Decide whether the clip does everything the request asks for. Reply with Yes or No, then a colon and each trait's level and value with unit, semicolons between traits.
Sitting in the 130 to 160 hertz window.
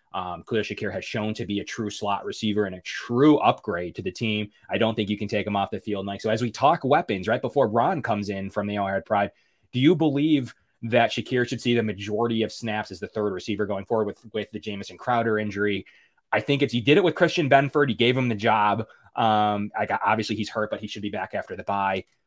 No: low, 105 Hz